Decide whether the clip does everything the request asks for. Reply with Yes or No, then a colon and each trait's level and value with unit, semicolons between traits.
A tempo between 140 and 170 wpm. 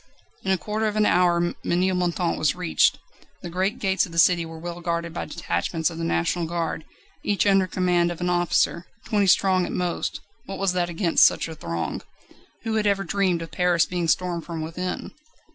No: average, 195 wpm